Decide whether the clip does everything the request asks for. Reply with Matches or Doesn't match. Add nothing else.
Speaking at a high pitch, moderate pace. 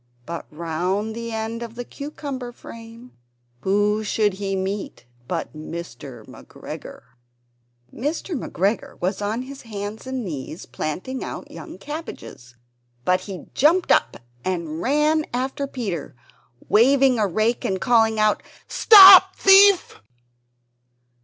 Doesn't match